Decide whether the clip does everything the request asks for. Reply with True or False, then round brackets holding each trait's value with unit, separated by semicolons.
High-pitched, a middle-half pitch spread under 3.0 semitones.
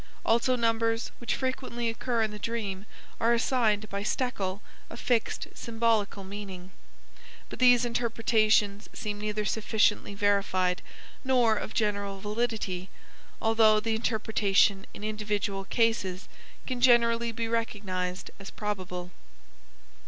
True (215 Hz; 2.5 semitones)